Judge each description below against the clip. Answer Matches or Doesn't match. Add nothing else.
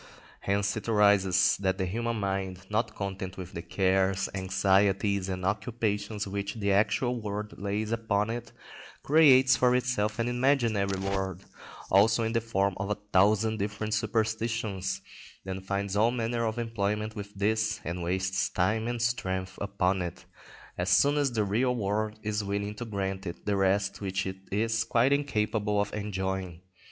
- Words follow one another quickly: Doesn't match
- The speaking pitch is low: Matches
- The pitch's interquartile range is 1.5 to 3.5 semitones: Matches